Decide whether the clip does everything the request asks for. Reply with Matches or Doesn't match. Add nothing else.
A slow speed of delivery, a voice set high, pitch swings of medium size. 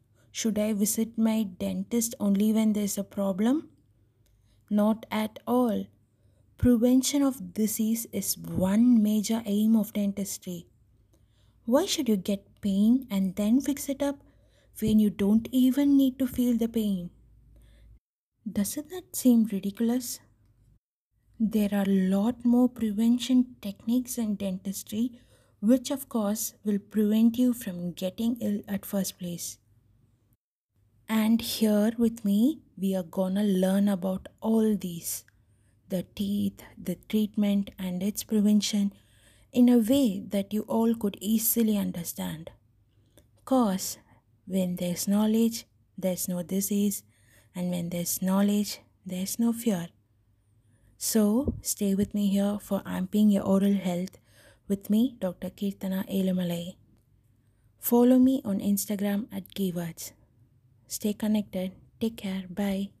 Matches